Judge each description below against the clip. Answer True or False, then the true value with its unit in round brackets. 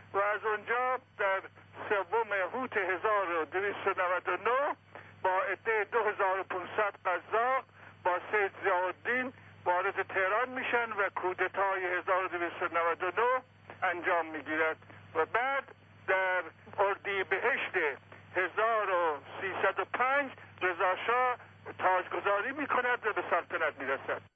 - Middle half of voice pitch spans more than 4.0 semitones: False (3.4 semitones)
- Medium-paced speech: False (85 wpm)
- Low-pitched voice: False (195 Hz)